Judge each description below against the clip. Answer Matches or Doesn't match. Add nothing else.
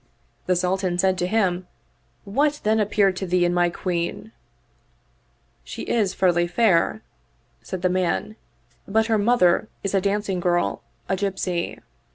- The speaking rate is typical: Matches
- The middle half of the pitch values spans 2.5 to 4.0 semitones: Matches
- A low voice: Doesn't match